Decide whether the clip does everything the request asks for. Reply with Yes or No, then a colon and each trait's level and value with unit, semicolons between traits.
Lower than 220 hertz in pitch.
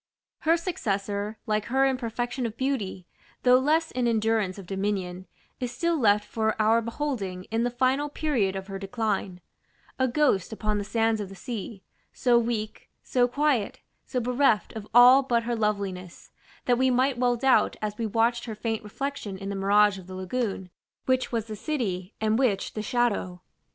No: high, 225 Hz